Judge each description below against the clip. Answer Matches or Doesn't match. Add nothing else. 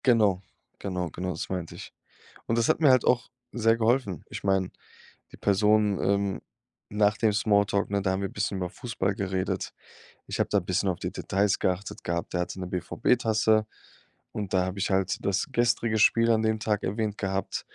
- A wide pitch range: Doesn't match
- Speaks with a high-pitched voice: Doesn't match